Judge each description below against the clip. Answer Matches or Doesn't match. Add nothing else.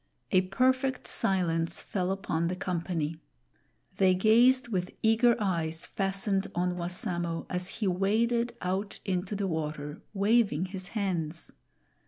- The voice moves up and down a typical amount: Matches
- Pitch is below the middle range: Doesn't match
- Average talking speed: Doesn't match